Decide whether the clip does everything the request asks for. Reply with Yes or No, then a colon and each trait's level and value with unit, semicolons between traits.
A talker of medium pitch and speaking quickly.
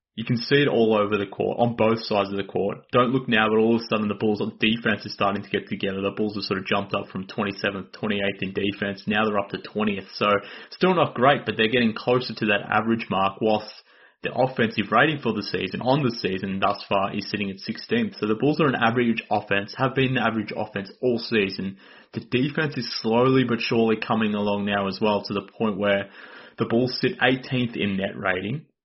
No: low, 110 Hz; fast, 235 wpm